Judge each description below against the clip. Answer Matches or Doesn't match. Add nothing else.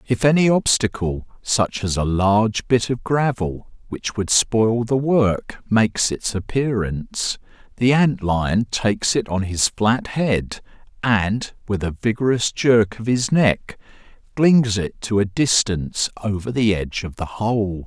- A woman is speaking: Doesn't match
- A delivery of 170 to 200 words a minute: Doesn't match